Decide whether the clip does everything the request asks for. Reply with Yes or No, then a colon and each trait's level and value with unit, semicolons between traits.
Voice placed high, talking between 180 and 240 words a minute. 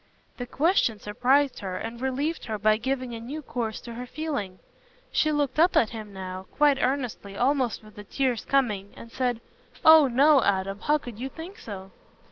Yes: high, 245 Hz; average, 185 wpm